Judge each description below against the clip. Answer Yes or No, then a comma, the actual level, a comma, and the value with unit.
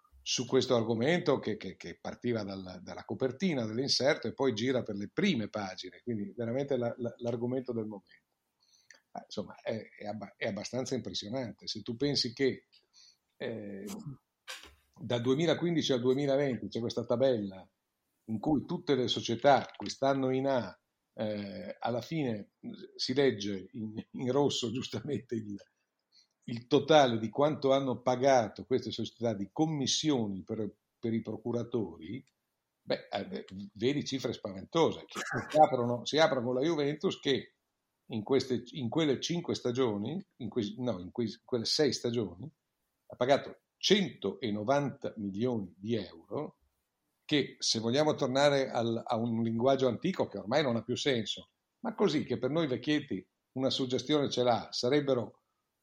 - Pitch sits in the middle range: No, low, 120 Hz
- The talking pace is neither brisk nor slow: Yes, average, 145 wpm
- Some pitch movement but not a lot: Yes, average, 3.4 semitones